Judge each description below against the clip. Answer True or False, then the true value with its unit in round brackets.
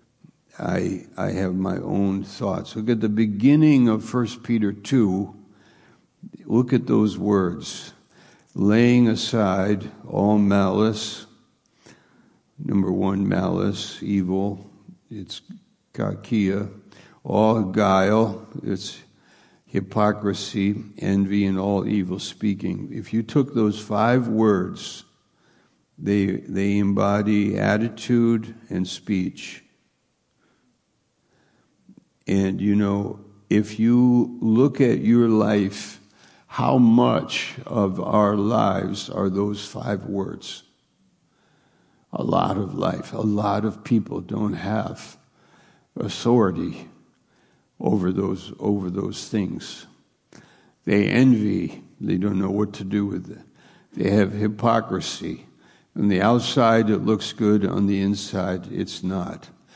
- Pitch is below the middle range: True (105 Hz)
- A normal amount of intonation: False (2.1 semitones)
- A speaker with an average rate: False (105 wpm)